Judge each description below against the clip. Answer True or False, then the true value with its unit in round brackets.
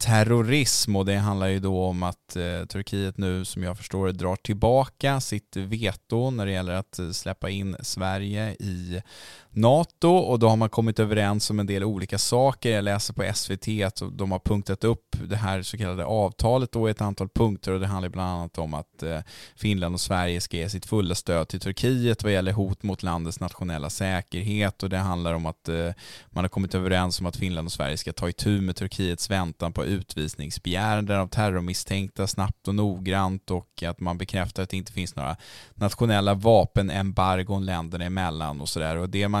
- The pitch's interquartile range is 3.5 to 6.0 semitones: False (2.7 semitones)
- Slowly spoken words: False (190 wpm)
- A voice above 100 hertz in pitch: False (95 Hz)